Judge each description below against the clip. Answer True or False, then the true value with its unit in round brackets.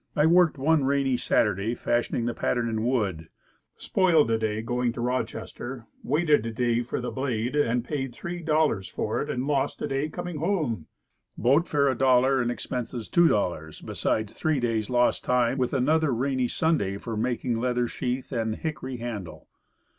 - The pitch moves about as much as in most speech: True (3.6 semitones)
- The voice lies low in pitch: True (125 Hz)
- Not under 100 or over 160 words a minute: False (170 wpm)